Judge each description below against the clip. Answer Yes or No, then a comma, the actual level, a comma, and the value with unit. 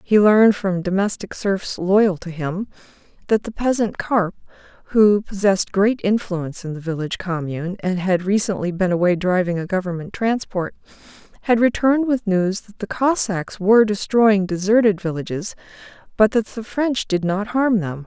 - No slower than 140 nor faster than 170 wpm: Yes, average, 160 wpm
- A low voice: No, high, 200 Hz